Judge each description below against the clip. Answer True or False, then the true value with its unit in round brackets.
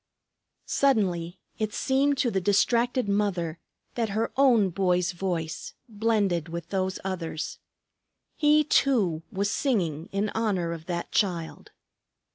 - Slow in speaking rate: True (120 wpm)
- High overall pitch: True (195 Hz)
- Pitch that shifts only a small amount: False (4.8 semitones)